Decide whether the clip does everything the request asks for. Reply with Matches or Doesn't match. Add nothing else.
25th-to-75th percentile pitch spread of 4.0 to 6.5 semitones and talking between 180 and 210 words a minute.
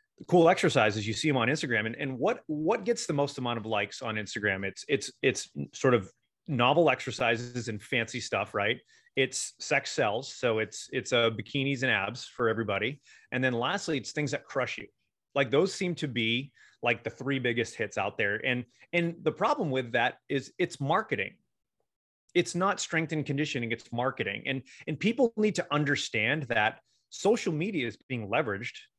Matches